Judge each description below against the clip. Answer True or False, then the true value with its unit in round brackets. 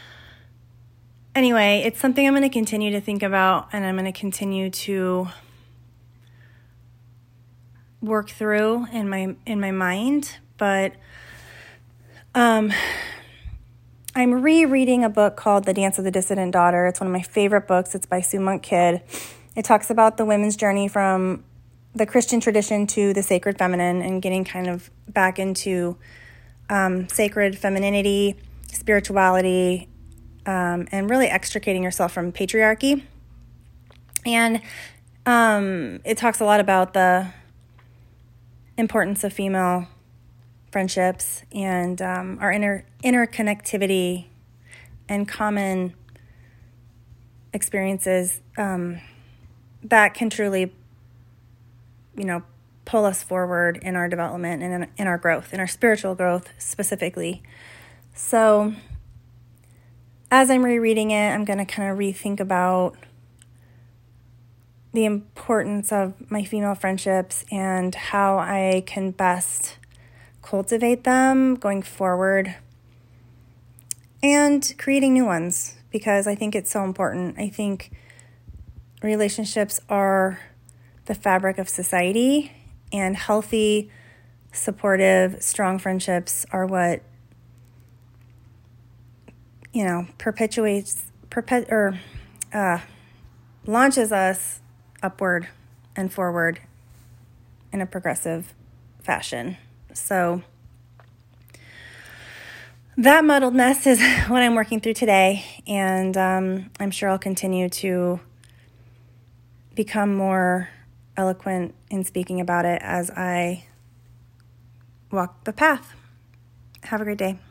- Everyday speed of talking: False (110 wpm)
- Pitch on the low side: False (185 Hz)